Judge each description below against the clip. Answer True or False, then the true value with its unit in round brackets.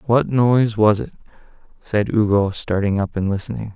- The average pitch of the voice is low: True (105 Hz)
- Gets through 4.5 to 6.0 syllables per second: True (5.1 syllables/s)